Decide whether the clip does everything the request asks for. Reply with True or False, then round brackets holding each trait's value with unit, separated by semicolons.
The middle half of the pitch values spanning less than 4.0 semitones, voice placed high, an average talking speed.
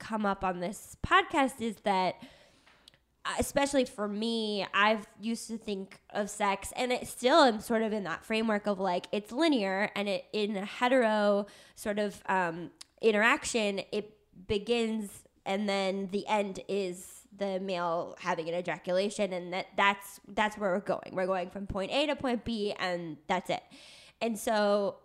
True (2.9 semitones; 205 Hz; 170 wpm)